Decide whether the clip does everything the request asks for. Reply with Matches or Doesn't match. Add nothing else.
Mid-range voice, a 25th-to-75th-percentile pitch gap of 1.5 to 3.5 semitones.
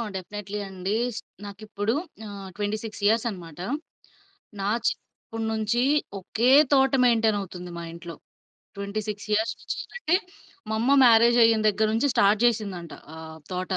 Doesn't match